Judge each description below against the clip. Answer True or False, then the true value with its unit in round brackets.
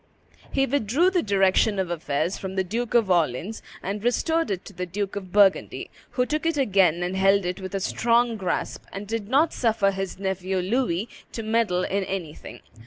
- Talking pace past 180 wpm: True (190 wpm)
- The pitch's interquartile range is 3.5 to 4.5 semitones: True (3.8 semitones)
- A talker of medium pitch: False (195 Hz)